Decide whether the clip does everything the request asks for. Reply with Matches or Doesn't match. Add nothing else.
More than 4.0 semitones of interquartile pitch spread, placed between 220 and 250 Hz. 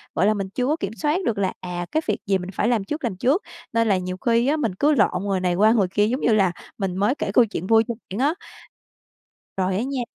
Doesn't match